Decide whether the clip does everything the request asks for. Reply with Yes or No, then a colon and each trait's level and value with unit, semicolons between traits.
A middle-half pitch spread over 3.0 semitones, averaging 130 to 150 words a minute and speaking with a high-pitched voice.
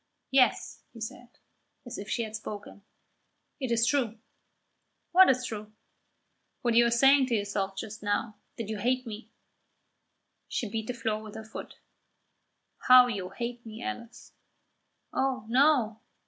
No: average, 2.7 semitones; average, 145 wpm; high, 230 Hz